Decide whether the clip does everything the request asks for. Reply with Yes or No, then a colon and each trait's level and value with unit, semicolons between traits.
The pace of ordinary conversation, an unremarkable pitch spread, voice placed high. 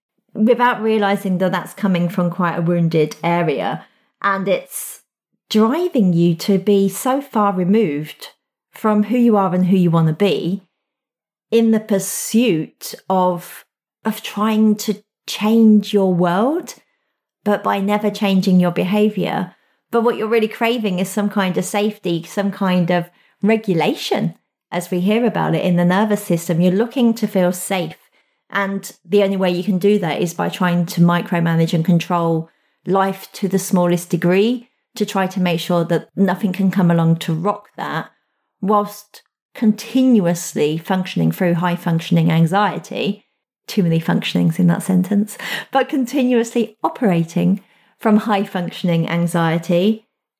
Yes: average, 150 wpm; average, 3.3 semitones; high, 195 Hz